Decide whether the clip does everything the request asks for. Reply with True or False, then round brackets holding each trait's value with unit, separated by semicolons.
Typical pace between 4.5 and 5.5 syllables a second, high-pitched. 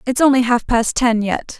True (4.8 syllables/s; 245 Hz)